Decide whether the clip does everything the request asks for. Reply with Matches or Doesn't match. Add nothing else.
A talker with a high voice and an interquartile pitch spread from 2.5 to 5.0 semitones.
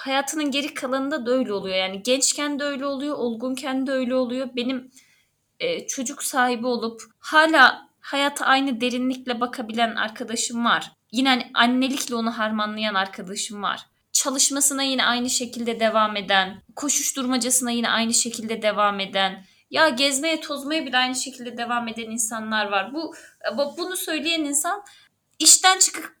Matches